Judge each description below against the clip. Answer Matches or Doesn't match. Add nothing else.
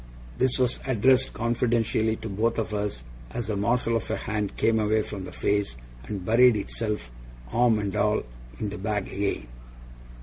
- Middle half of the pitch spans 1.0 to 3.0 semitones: Matches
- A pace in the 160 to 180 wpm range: Matches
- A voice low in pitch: Matches